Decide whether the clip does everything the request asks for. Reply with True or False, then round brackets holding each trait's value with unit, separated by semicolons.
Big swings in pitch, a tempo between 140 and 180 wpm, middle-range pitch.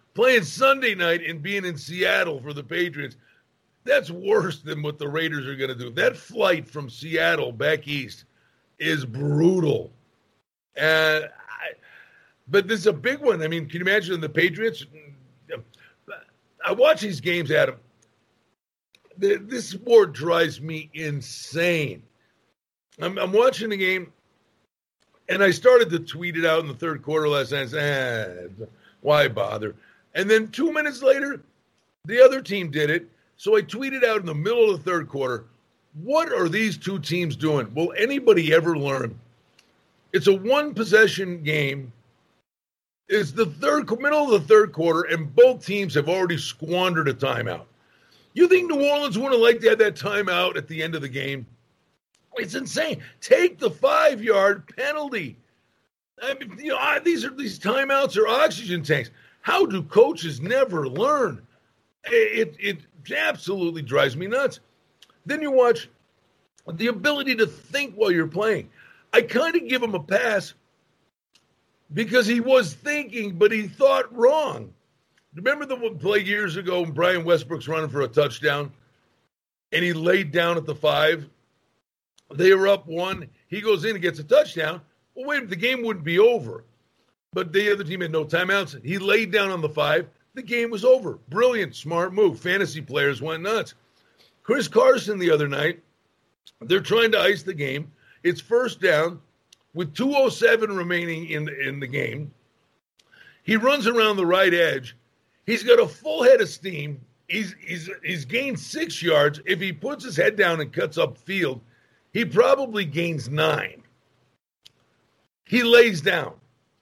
True (8.2 semitones; 165 wpm; 180 Hz)